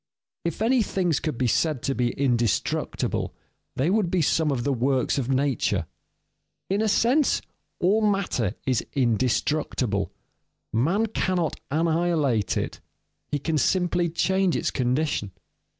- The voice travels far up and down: Yes, wide, 6.1 semitones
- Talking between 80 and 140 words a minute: Yes, slow, 135 wpm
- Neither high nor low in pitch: Yes, medium, 155 Hz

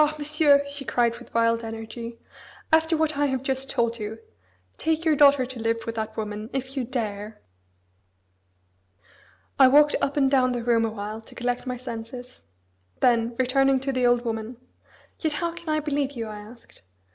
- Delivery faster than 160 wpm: Yes, average, 175 wpm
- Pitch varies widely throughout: No, average, 3.6 semitones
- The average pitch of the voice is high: Yes, very high, 250 Hz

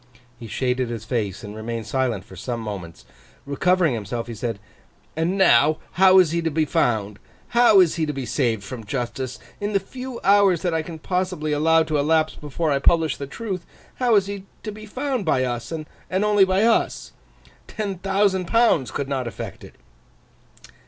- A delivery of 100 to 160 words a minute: No, average, 185 wpm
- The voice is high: No, medium, 155 Hz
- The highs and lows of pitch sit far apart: Yes, wide, 7.8 semitones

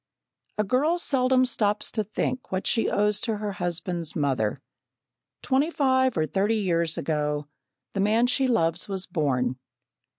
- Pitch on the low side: No, high, 205 Hz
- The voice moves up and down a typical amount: No, wide, 7.1 semitones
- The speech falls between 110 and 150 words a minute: Yes, average, 145 wpm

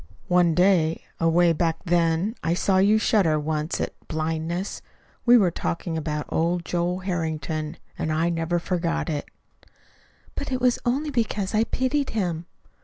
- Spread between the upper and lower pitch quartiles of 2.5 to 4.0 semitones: Yes, average, 3.4 semitones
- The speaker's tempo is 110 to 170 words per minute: Yes, average, 150 wpm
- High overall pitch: No, medium, 170 Hz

